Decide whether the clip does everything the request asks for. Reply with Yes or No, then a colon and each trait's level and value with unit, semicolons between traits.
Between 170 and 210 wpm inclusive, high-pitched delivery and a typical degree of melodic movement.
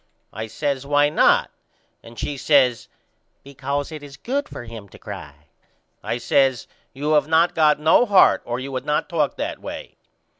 No: average, 175 wpm; medium, 140 Hz; average, 3.2 semitones